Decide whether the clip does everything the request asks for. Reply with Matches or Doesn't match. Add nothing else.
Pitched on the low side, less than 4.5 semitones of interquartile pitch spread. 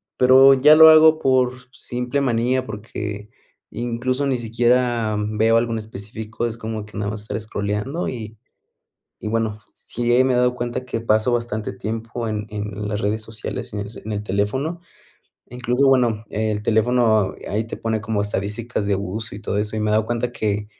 Matches